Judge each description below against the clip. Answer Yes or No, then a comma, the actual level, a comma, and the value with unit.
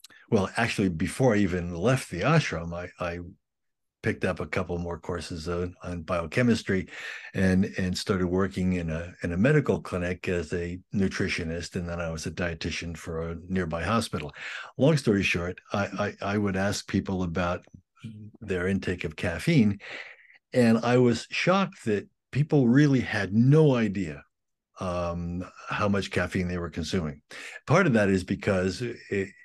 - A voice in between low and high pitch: No, very low, 95 Hz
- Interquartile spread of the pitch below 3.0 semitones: No, average, 3.3 semitones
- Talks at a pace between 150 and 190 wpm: Yes, average, 160 wpm